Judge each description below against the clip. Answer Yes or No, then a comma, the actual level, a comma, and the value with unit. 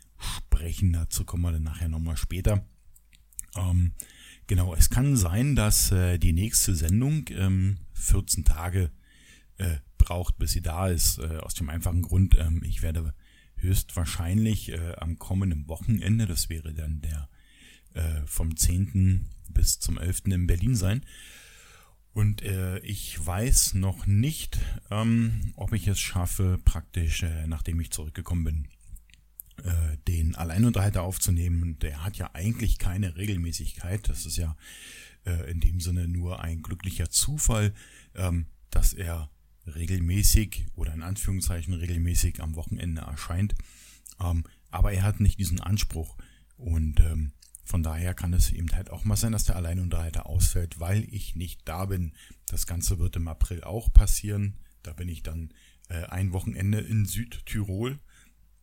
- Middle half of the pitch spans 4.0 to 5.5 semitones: No, average, 3.1 semitones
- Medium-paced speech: Yes, average, 140 wpm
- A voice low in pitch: Yes, very low, 90 Hz